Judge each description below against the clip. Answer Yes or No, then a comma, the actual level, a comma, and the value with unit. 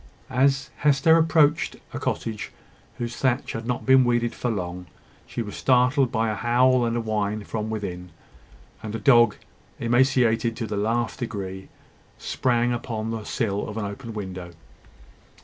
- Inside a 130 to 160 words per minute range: Yes, average, 150 wpm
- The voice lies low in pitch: Yes, low, 115 Hz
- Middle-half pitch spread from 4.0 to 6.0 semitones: No, average, 2.9 semitones